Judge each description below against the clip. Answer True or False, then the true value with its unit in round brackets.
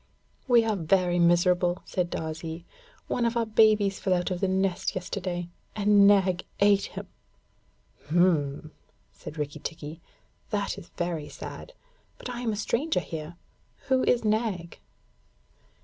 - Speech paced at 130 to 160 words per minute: True (140 wpm)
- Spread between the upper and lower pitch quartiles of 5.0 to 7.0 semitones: False (3.6 semitones)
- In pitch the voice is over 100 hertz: True (185 Hz)